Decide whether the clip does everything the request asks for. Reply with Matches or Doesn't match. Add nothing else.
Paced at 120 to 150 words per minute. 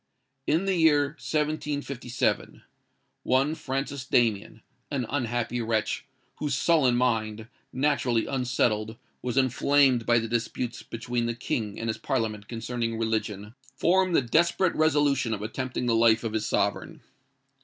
Matches